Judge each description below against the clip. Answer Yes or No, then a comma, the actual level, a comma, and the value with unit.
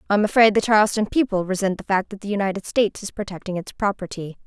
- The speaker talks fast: Yes, fast, 230 wpm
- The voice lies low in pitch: No, high, 200 Hz